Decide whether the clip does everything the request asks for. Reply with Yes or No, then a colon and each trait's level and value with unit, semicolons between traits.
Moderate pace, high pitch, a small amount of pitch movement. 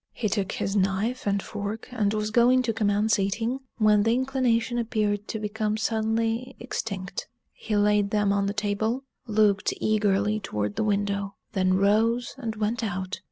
Yes: average, 160 wpm; high, 210 Hz; narrow, 2.1 semitones